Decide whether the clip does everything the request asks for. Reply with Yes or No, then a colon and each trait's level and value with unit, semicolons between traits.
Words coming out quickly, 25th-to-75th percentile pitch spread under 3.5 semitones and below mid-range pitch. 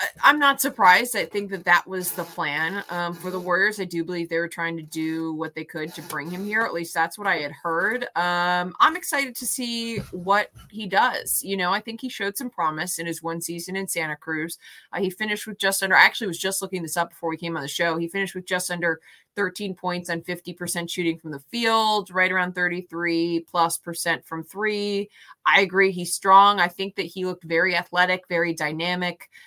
No: fast, 225 wpm; average, 2.8 semitones; medium, 180 Hz